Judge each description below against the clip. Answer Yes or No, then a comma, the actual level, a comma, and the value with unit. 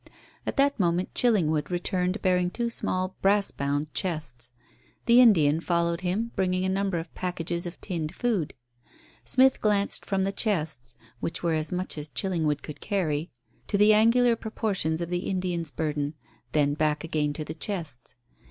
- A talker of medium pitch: Yes, medium, 175 Hz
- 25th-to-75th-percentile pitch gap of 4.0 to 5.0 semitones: Yes, average, 4.3 semitones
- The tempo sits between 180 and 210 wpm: No, average, 160 wpm